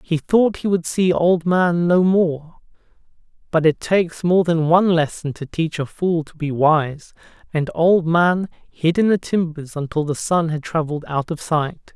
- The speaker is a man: Yes, male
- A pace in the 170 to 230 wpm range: Yes, average, 190 wpm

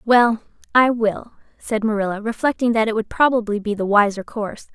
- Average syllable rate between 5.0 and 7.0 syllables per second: Yes, 5.5 syllables/s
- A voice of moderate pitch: No, high, 220 Hz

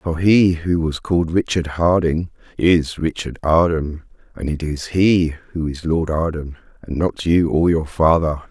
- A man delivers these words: Yes, male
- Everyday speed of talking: Yes, average, 170 wpm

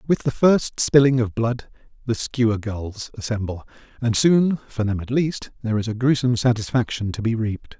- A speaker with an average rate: Yes, average, 185 wpm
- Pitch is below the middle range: Yes, low, 120 Hz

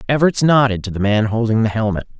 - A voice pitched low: Yes, low, 115 Hz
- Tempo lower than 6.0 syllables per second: No, 6.2 syllables/s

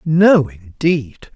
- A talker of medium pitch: Yes, medium, 145 Hz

